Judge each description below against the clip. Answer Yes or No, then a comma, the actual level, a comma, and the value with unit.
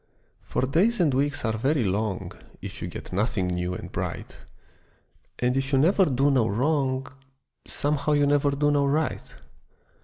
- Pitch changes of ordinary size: Yes, average, 4.0 semitones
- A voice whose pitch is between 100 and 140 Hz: Yes, low, 135 Hz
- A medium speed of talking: Yes, average, 160 wpm